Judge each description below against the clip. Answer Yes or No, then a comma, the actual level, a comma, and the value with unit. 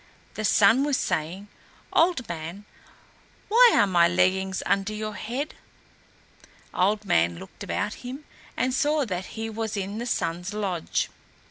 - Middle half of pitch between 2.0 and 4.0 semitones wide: No, average, 4.7 semitones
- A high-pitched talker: Yes, high, 205 Hz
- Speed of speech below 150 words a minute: Yes, average, 140 wpm